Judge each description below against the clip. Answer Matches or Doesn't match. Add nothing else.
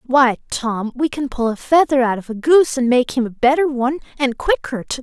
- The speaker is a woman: Matches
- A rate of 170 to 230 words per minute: Doesn't match